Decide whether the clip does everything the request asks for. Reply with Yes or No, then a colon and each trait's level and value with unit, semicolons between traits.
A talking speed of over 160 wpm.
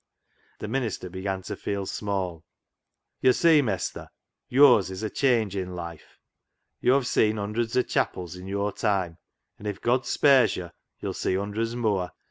No: average, 155 wpm